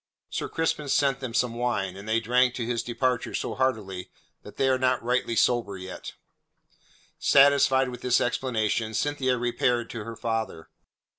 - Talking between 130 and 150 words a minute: No, average, 160 wpm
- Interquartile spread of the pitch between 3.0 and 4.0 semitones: No, narrow, 2.4 semitones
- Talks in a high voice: No, low, 120 Hz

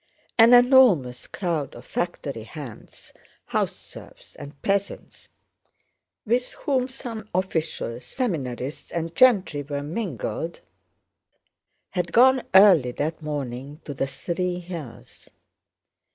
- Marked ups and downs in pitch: Yes, wide, 7.1 semitones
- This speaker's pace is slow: Yes, slow, 105 wpm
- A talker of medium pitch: Yes, medium, 165 Hz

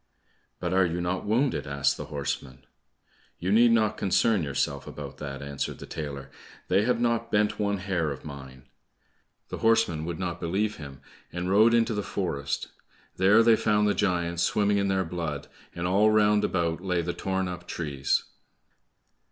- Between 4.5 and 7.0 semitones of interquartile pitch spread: Yes, wide, 5.6 semitones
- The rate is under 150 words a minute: No, average, 170 wpm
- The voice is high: No, very low, 90 Hz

